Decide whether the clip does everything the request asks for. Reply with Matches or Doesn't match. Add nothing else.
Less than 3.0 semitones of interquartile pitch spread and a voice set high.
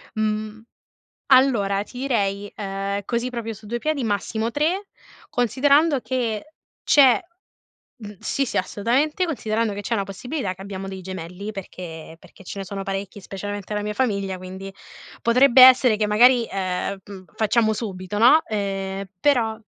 Doesn't match